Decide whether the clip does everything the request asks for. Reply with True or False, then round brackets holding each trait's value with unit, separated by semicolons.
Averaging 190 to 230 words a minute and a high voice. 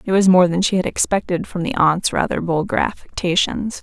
False (205 wpm; 180 Hz)